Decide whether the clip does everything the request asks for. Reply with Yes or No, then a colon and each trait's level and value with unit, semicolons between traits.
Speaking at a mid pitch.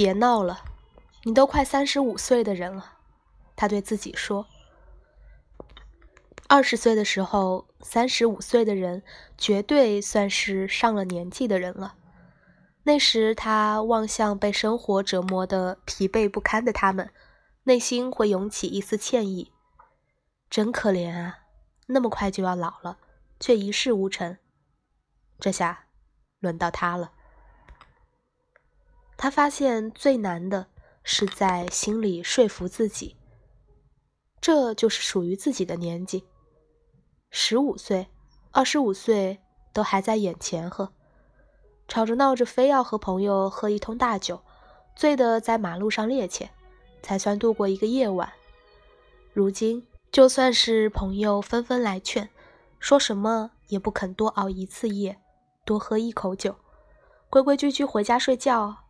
No: high, 210 Hz